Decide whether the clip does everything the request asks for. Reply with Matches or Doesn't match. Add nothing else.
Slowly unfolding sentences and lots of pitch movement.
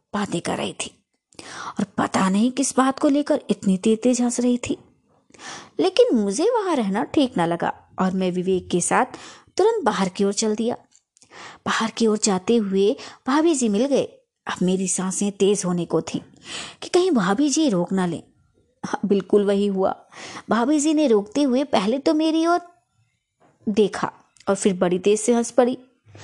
Doesn't match